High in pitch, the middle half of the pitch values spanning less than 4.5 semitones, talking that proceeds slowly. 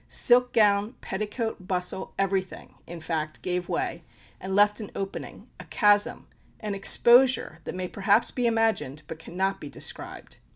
No: high, 195 Hz; average, 3.2 semitones; average, 150 wpm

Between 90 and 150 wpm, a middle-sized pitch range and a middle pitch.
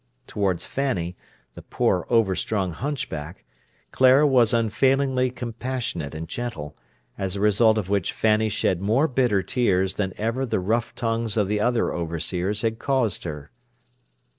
No: average, 140 wpm; average, 4.7 semitones; low, 110 Hz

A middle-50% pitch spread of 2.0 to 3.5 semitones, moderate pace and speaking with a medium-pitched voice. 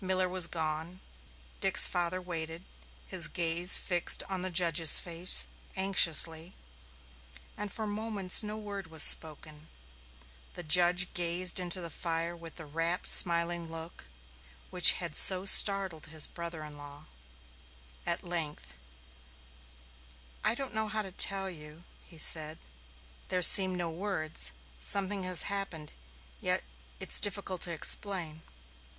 No: narrow, 2.6 semitones; slow, 130 wpm; medium, 175 Hz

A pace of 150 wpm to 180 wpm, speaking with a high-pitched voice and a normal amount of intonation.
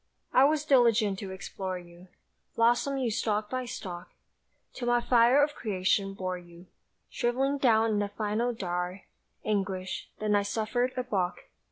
Yes: average, 155 wpm; high, 215 Hz; average, 4.4 semitones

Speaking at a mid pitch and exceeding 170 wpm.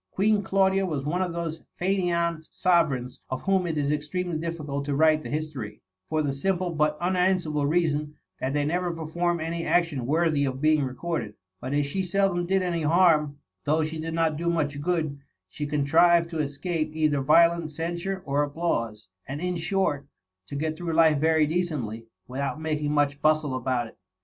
Yes: medium, 155 Hz; average, 180 wpm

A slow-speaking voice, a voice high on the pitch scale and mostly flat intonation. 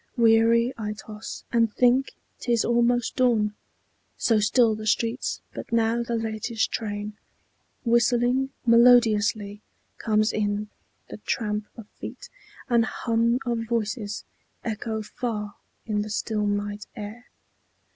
Yes: slow, 125 wpm; high, 225 Hz; narrow, 2.0 semitones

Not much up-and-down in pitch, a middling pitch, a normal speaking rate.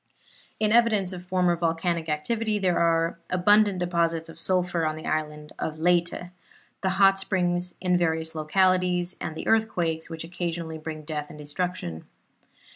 Yes: narrow, 2.3 semitones; medium, 175 Hz; average, 150 wpm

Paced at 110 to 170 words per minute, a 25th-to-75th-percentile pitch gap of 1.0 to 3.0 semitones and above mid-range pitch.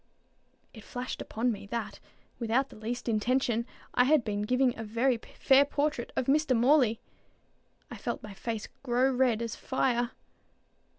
Yes: average, 160 wpm; average, 2.7 semitones; high, 240 Hz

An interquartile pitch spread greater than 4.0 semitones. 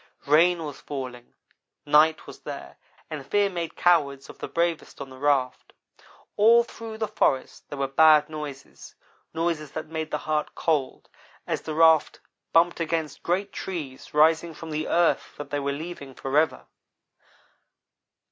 No: average, 3.0 semitones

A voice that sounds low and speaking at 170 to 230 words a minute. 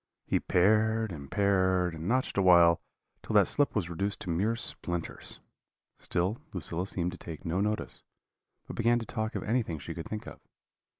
Yes: very low, 95 Hz; average, 175 wpm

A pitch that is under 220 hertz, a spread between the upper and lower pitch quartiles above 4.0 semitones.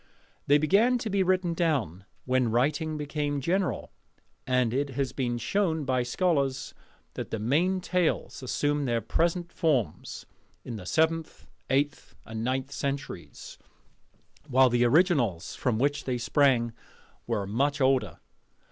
Yes: medium, 140 Hz; average, 4.8 semitones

